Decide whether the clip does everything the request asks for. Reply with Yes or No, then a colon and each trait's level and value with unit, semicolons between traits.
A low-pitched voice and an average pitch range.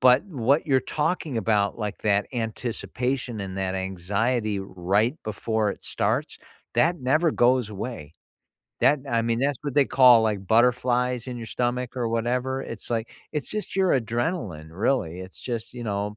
Yes: low, 120 Hz; average, 3.7 semitones